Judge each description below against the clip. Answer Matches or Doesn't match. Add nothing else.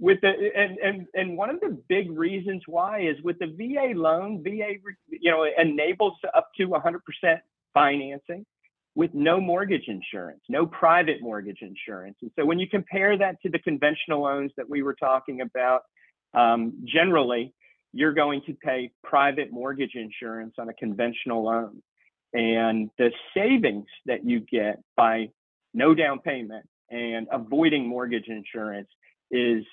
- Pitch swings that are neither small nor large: Doesn't match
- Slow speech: Doesn't match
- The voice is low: Doesn't match